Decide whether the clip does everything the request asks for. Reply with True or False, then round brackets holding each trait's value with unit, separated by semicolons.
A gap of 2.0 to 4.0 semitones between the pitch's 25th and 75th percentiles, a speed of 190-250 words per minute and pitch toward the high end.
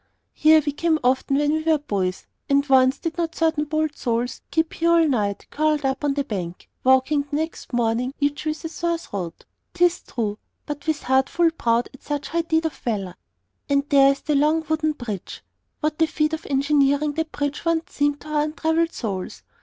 True (3.2 semitones; 200 wpm; 290 Hz)